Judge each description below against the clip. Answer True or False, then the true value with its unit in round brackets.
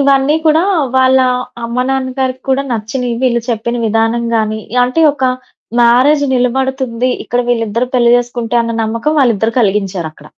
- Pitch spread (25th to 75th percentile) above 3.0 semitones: False (2.6 semitones)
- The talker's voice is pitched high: True (245 Hz)